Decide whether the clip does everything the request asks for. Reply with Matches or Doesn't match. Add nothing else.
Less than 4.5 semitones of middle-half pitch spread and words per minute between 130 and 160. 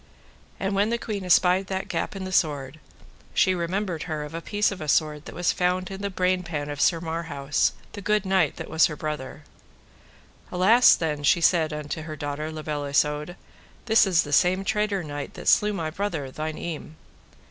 Doesn't match